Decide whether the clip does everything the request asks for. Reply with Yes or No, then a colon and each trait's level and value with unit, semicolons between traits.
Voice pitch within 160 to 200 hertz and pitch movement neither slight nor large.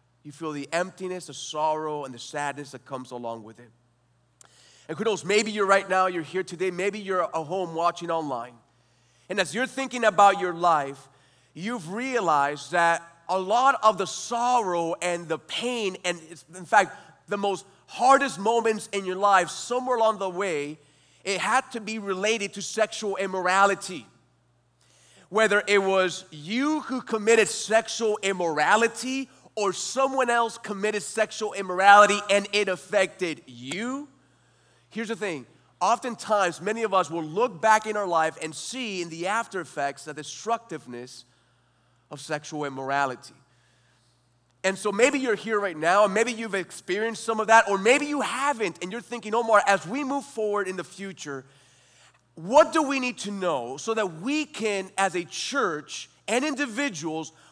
No: high, 190 Hz; wide, 6.1 semitones